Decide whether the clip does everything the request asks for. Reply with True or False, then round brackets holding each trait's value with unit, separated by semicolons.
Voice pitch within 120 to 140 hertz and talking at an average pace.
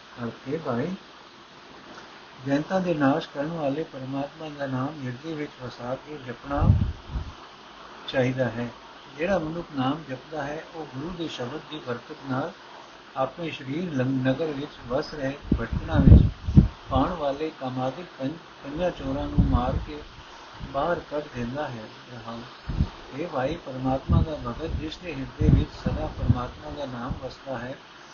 True (135 Hz; 135 wpm)